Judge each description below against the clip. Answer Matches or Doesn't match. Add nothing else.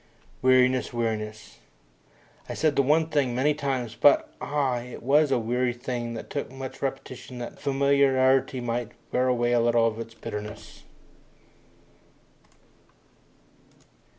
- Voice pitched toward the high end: Doesn't match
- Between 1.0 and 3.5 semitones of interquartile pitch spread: Matches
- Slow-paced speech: Matches